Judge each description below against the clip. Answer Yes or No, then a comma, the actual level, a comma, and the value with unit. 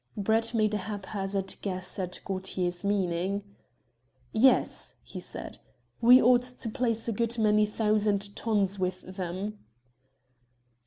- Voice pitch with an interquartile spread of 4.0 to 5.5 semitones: No, average, 2.8 semitones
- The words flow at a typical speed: No, slow, 120 wpm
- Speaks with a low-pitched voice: No, high, 205 Hz